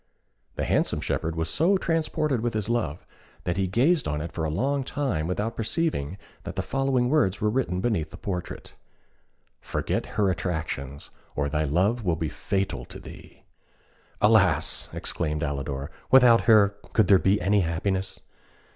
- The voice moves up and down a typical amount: No, wide, 6.8 semitones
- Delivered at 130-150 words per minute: No, average, 160 wpm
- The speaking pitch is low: Yes, very low, 95 Hz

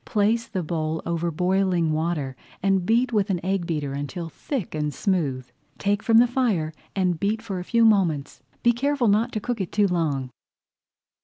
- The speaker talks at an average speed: Yes, average, 180 wpm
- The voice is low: No, high, 190 Hz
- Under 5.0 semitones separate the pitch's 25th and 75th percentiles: No, wide, 5.5 semitones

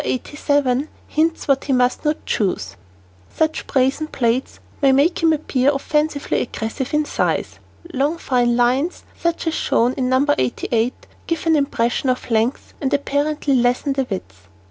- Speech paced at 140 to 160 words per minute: Yes, average, 150 wpm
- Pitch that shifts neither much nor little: Yes, average, 3.4 semitones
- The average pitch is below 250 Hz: No, very high, 270 Hz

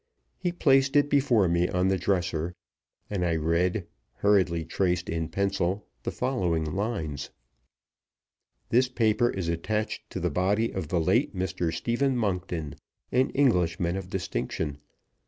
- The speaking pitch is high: No, very low, 95 Hz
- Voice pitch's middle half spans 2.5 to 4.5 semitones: No, average, 4.9 semitones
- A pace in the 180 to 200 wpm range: No, average, 140 wpm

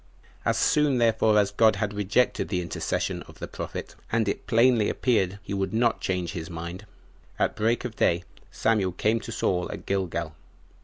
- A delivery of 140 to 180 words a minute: Yes, average, 175 wpm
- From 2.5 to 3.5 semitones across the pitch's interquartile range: No, average, 3.9 semitones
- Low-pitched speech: Yes, low, 105 Hz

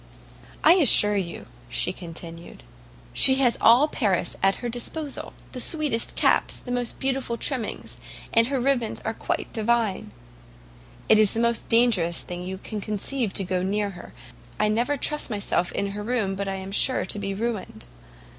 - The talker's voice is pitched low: No, high, 220 Hz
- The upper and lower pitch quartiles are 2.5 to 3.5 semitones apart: No, average, 4.2 semitones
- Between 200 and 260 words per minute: No, average, 170 wpm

